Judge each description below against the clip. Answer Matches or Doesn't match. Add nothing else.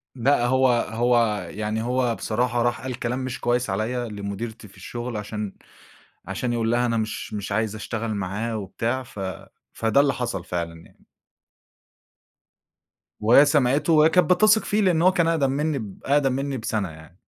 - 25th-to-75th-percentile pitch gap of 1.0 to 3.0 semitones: Doesn't match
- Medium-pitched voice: Doesn't match